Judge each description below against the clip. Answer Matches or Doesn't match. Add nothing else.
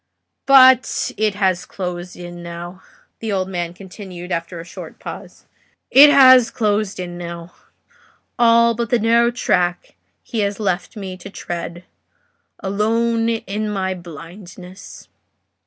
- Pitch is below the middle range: Doesn't match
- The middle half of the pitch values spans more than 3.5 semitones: Matches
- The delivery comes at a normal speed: Doesn't match